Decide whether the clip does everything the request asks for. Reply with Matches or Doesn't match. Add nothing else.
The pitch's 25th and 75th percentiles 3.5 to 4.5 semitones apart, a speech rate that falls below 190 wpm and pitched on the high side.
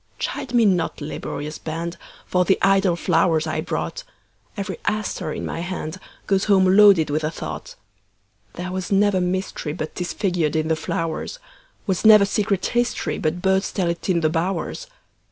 Doesn't match